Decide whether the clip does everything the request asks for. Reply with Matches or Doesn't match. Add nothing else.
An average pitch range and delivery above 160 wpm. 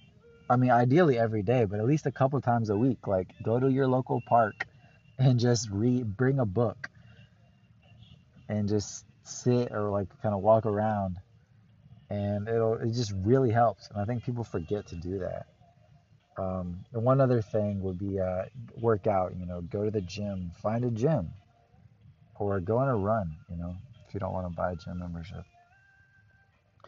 Matches